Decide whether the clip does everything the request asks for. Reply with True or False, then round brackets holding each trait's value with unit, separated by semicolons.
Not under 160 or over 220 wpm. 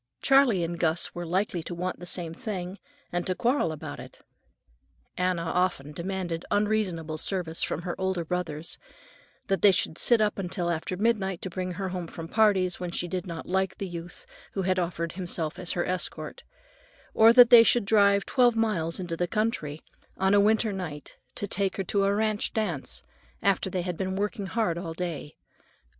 True (185 wpm)